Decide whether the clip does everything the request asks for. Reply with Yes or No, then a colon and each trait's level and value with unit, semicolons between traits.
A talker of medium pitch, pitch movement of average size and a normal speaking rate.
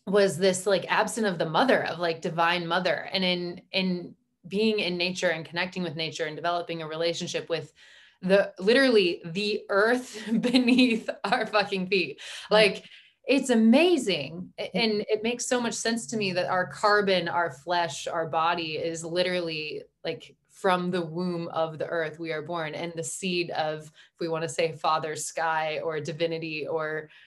Yes: medium, 180 Hz; average, 4.0 semitones; average, 170 wpm